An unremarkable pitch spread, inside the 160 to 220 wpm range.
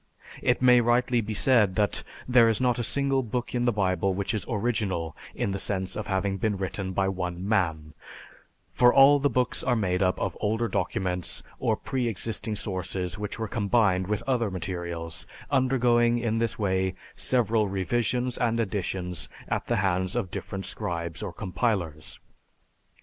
Yes: average, 4.3 semitones; average, 165 wpm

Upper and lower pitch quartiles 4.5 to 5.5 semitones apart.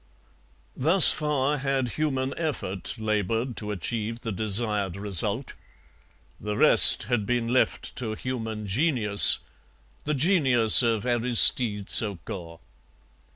No: average, 3.9 semitones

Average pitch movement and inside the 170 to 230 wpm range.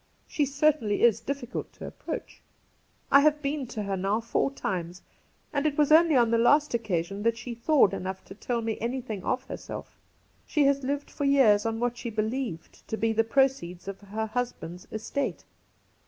Yes: average, 4.9 semitones; average, 185 wpm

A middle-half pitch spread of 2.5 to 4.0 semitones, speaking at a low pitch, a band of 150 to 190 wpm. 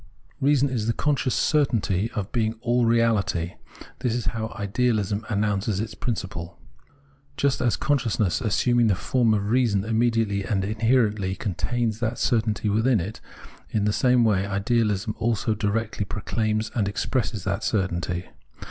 No: average, 2.9 semitones; low, 110 Hz; average, 140 wpm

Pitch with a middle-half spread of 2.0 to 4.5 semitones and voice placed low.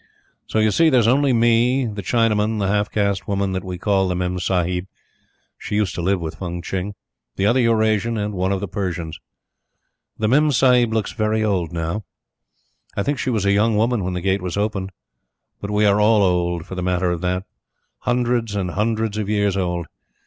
Yes: average, 3.4 semitones; low, 100 Hz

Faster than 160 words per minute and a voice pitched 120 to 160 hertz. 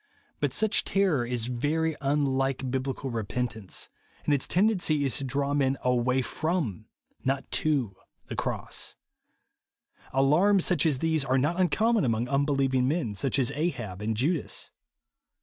No: average, 150 wpm; low, 135 Hz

